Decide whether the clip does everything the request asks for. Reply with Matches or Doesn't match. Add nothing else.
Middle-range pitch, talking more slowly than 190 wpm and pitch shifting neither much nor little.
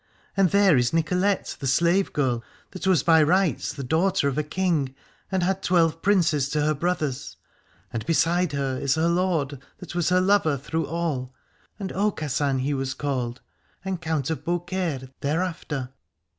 Matches